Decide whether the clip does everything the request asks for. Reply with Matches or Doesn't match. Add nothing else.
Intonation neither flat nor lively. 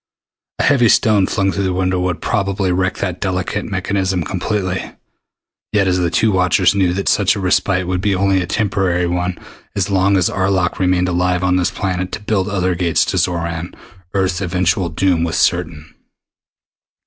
Doesn't match